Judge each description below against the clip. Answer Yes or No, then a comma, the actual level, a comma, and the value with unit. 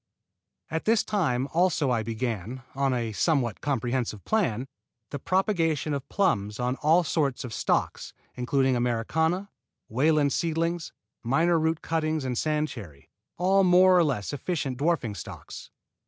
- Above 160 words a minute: No, average, 140 wpm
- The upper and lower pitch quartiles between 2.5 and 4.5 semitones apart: No, average, 5.2 semitones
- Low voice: No, medium, 145 Hz